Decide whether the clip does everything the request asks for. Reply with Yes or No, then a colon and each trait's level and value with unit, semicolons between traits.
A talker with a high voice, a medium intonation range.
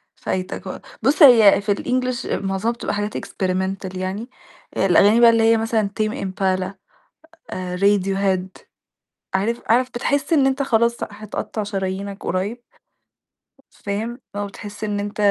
Yes: high, 205 Hz; average, 3.3 semitones